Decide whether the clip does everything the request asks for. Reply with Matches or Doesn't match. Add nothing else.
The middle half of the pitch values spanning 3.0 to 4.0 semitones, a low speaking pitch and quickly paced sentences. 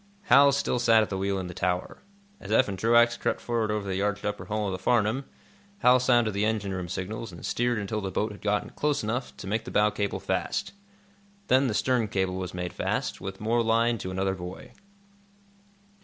Matches